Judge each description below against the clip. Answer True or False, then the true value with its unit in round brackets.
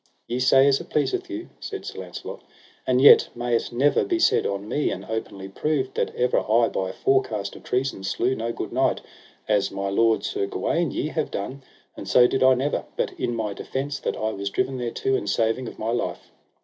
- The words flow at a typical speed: False (215 wpm)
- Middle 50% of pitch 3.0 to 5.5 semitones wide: True (4.1 semitones)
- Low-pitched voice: True (125 Hz)